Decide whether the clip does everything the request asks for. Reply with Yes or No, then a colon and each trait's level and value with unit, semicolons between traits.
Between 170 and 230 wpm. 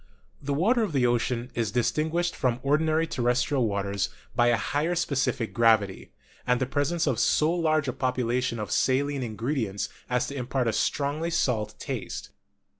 No: average, 160 wpm